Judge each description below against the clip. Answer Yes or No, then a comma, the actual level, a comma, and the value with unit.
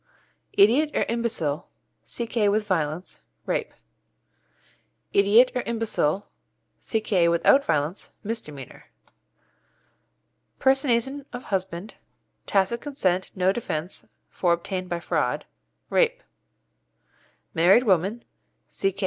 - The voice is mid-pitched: No, high, 200 Hz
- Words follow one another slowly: Yes, slow, 90 wpm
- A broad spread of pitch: No, average, 5.0 semitones